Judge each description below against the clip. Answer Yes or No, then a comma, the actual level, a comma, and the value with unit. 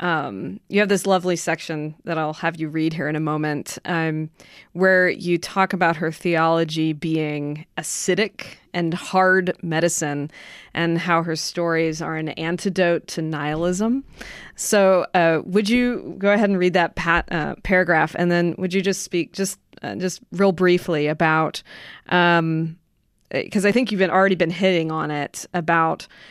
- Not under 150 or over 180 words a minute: Yes, average, 165 wpm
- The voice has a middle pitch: Yes, medium, 170 Hz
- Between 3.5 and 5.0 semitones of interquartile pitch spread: No, narrow, 2.6 semitones